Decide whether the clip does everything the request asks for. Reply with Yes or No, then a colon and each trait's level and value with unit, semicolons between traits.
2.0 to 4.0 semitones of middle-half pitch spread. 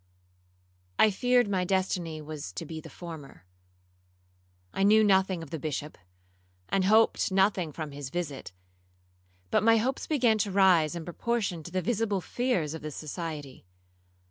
No: average, 4.9 semitones